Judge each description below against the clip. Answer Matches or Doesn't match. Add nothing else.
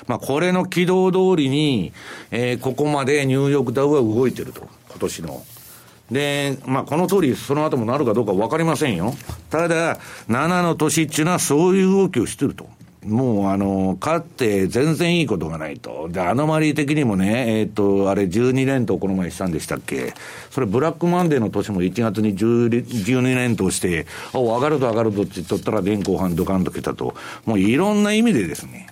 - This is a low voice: Matches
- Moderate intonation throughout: Doesn't match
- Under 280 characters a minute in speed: Doesn't match